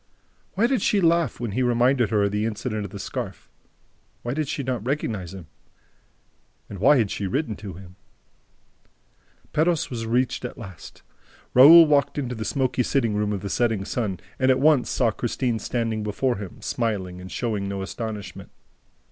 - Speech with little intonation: No, average, 4.3 semitones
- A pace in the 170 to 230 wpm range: Yes, average, 175 wpm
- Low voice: Yes, low, 115 Hz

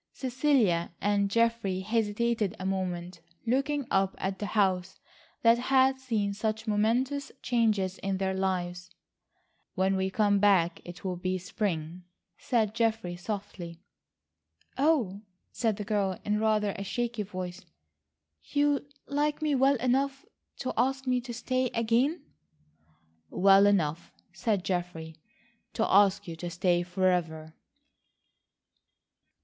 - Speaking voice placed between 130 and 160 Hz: No, high, 205 Hz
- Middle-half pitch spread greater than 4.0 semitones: Yes, average, 4.4 semitones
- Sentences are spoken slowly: Yes, slow, 125 wpm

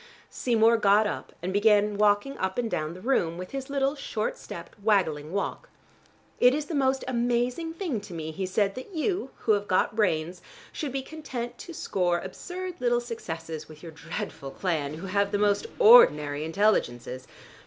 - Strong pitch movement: Yes, wide, 6.8 semitones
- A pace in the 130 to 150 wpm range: No, average, 175 wpm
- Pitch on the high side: Yes, high, 210 Hz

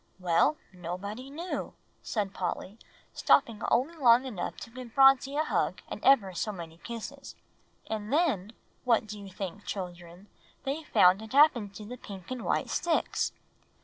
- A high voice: Yes, high, 220 Hz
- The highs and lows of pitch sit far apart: Yes, wide, 6.0 semitones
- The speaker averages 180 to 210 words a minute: No, average, 160 wpm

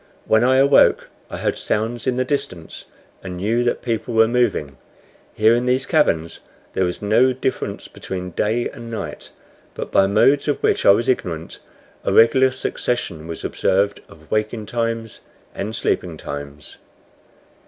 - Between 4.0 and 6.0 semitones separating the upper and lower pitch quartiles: Yes, average, 5.1 semitones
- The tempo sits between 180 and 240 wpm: No, average, 155 wpm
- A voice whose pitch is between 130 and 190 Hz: No, low, 110 Hz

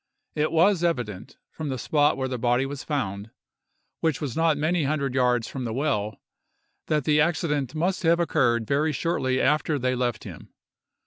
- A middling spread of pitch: Yes, average, 3.9 semitones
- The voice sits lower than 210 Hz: Yes, medium, 140 Hz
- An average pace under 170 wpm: No, average, 175 wpm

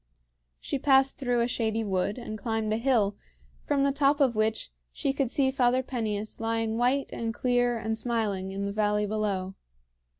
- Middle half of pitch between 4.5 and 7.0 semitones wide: No, average, 3.3 semitones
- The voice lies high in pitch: Yes, high, 225 Hz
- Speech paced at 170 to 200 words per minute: Yes, average, 175 wpm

